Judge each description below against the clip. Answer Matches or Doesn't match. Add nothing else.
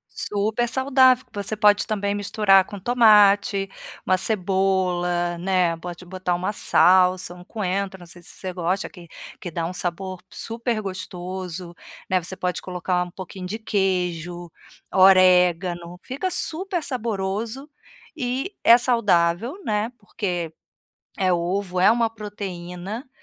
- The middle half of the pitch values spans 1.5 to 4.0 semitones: Matches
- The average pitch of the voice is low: Doesn't match